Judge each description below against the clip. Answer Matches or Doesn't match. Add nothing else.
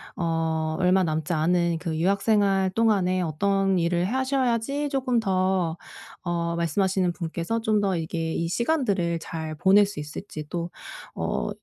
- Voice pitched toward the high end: Doesn't match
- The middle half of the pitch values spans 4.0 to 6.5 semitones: Doesn't match